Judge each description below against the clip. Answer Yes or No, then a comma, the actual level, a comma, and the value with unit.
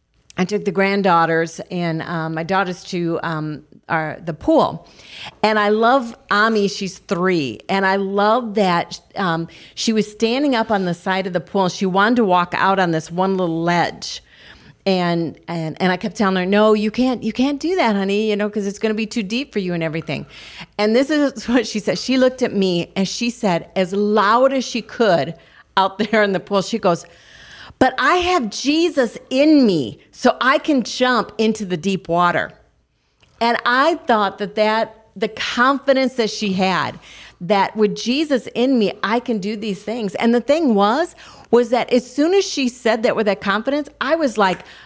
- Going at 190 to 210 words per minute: Yes, average, 200 wpm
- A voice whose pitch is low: No, high, 210 Hz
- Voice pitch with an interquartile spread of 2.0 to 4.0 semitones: No, average, 4.4 semitones